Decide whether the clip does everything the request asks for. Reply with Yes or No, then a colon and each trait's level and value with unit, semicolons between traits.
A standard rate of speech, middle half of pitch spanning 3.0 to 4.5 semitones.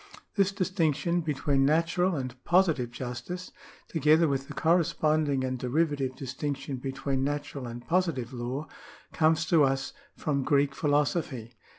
No: slow, 125 wpm; average, 3.6 semitones